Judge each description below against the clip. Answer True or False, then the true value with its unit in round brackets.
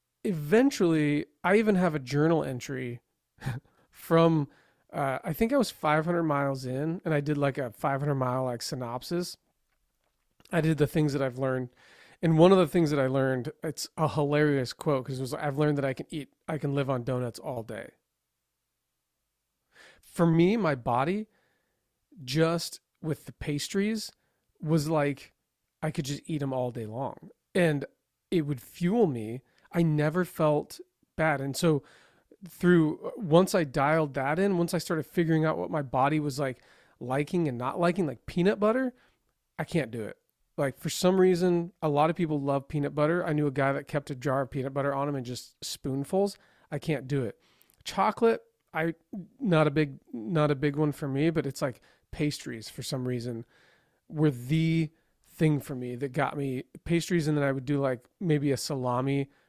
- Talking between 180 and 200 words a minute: True (185 wpm)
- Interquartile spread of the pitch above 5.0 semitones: False (3.6 semitones)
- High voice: False (150 Hz)